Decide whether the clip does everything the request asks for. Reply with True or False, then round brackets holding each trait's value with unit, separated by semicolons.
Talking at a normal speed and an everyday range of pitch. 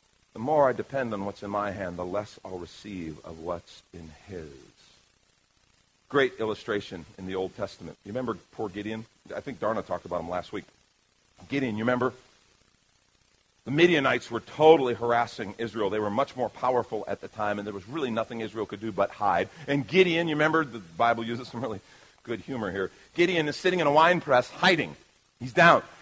True (195 wpm; 4.2 semitones)